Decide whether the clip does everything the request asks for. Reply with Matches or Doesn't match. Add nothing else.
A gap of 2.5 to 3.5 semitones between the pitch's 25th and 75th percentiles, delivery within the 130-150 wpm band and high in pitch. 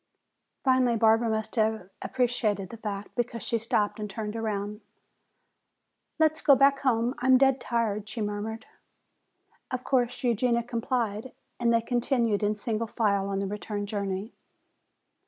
Matches